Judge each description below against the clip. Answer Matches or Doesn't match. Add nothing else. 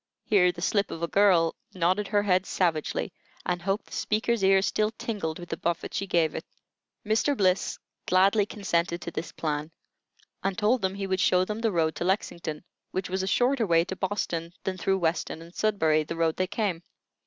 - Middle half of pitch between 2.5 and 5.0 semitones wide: Matches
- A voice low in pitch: Doesn't match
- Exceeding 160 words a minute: Matches